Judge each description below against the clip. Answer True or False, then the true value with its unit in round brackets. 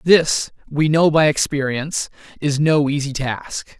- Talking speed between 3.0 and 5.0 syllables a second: True (4.1 syllables/s)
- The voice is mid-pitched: True (145 Hz)